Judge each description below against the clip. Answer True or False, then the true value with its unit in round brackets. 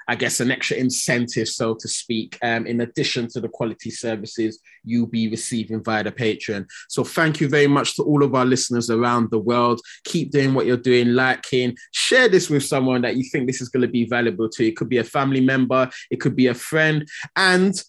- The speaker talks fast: True (225 wpm)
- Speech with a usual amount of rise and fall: True (3.2 semitones)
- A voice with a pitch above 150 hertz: False (125 Hz)